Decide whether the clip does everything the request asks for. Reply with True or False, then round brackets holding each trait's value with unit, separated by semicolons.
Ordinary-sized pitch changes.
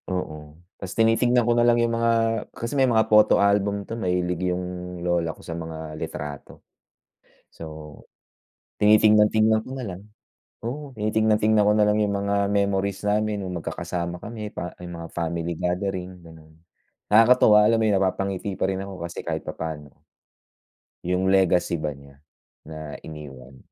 True (4.1 semitones)